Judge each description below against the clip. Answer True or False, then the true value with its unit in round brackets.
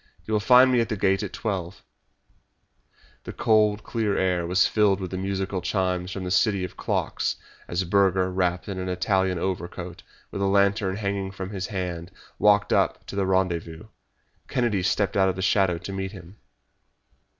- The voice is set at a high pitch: False (95 Hz)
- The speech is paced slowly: False (180 wpm)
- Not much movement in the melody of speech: True (1.8 semitones)